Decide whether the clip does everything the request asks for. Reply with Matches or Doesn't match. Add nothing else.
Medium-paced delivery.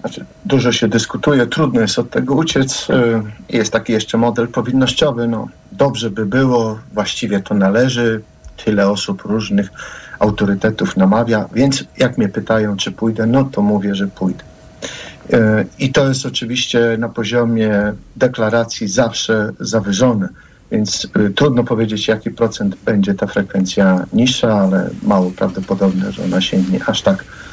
Matches